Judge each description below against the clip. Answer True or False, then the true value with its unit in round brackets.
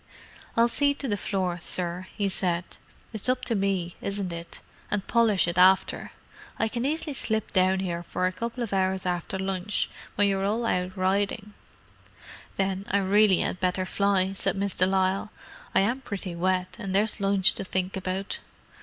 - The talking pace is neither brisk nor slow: True (180 wpm)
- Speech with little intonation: True (2.0 semitones)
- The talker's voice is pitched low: False (195 Hz)